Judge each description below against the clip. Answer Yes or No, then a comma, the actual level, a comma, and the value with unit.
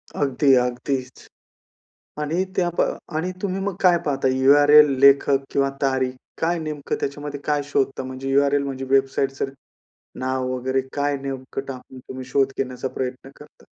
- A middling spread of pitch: No, narrow, 1.8 semitones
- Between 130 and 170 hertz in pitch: Yes, low, 135 Hz